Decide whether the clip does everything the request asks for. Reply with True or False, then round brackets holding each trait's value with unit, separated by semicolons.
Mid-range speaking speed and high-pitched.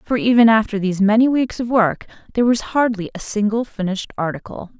True (190 wpm; 215 Hz)